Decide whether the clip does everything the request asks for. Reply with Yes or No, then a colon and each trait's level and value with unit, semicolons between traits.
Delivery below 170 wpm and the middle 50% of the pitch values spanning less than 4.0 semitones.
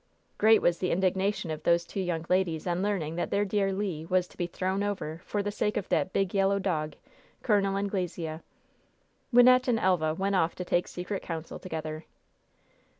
No: average, 185 wpm; average, 3.0 semitones